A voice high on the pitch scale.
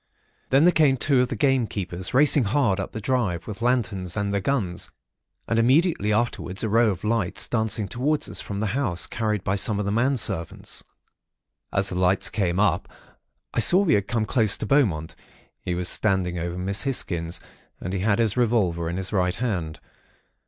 No: low, 105 Hz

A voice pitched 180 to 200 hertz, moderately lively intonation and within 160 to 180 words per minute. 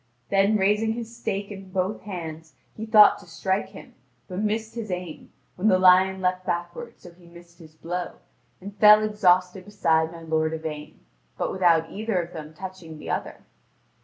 Yes: medium, 185 Hz; average, 3.4 semitones; average, 175 wpm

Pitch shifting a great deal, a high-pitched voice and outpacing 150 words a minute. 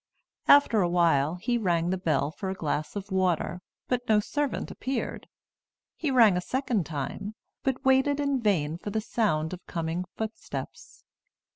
Yes: wide, 6.4 semitones; high, 195 Hz; average, 160 wpm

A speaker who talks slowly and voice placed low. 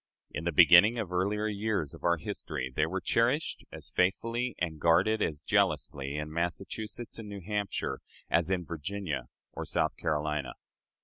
No: average, 160 wpm; very low, 90 Hz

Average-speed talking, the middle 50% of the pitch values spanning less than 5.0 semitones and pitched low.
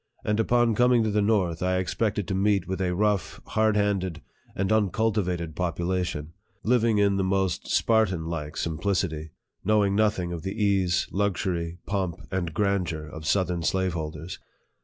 Yes: average, 160 wpm; average, 3.3 semitones; very low, 95 Hz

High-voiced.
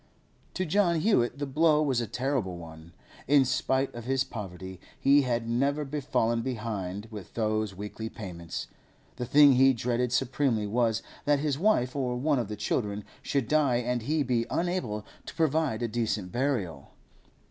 No: low, 125 Hz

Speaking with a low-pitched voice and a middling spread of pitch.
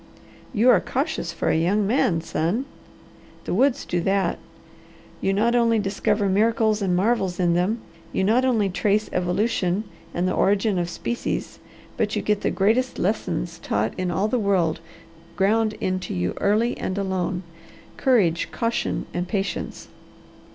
No: high, 200 Hz; average, 3.8 semitones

